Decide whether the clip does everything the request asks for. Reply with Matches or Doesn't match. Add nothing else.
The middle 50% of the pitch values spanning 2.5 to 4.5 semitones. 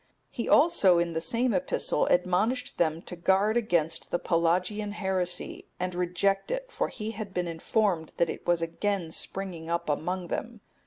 Matches